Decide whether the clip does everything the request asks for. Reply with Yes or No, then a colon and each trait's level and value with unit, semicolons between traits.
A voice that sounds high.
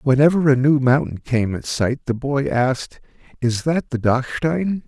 No: low, 135 Hz